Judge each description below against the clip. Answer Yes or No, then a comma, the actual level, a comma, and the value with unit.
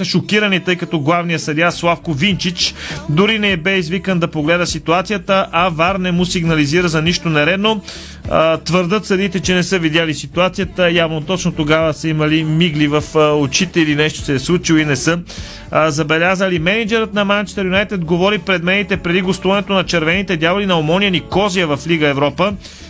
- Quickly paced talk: Yes, fast, 170 wpm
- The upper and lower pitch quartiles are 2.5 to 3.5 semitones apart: Yes, average, 3.0 semitones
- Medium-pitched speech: Yes, medium, 175 Hz